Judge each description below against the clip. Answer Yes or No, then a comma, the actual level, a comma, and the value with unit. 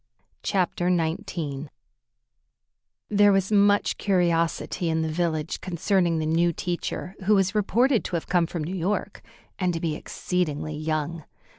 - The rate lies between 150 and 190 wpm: No, average, 140 wpm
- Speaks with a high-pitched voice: No, medium, 175 Hz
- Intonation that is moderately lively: Yes, average, 3.1 semitones